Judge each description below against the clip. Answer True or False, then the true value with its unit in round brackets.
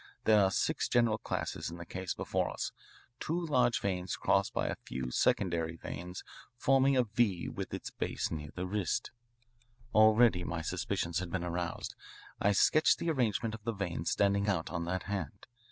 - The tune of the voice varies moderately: True (4.6 semitones)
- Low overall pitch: True (95 Hz)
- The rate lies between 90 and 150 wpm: False (175 wpm)